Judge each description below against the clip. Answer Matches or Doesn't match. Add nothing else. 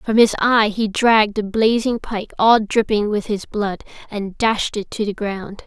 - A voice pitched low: Doesn't match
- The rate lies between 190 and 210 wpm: Matches